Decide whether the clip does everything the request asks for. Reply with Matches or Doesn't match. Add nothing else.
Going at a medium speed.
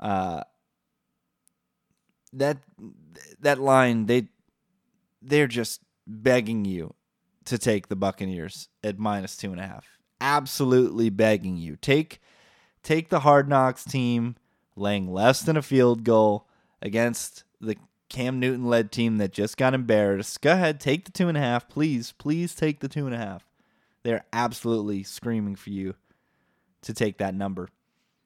Matches